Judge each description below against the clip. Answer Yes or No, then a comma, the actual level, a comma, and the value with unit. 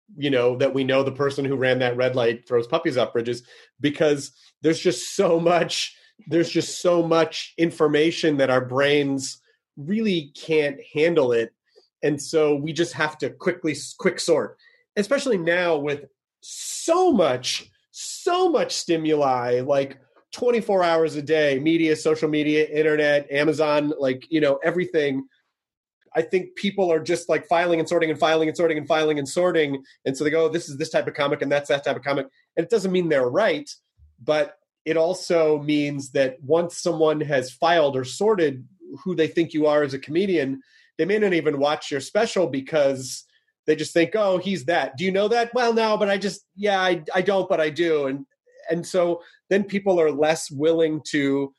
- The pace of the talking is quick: No, average, 190 wpm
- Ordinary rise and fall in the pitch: Yes, average, 3.8 semitones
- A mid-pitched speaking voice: Yes, medium, 160 Hz